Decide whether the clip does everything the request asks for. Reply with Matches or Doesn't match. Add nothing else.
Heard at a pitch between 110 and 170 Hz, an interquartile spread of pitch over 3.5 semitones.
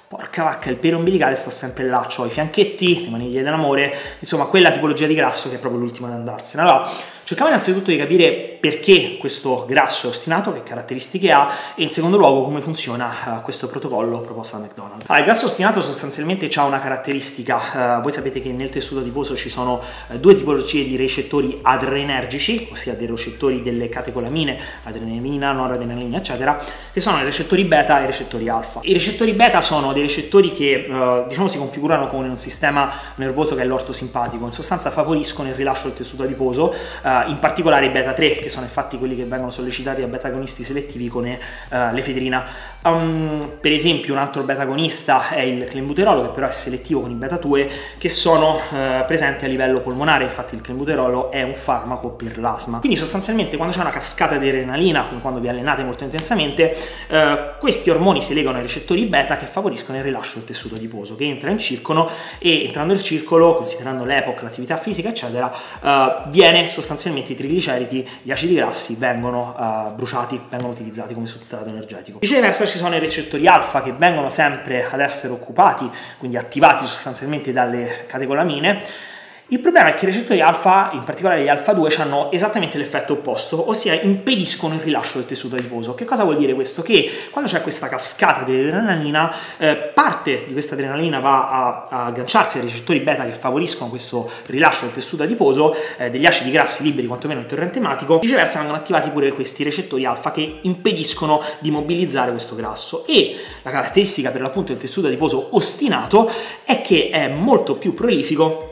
Matches